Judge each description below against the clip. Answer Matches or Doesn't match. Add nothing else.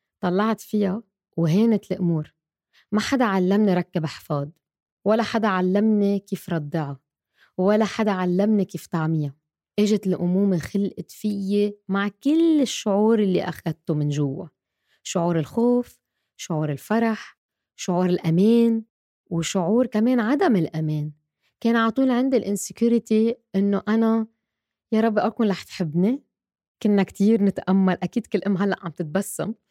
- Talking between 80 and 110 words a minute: Doesn't match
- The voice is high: Matches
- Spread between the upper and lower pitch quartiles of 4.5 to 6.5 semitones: Doesn't match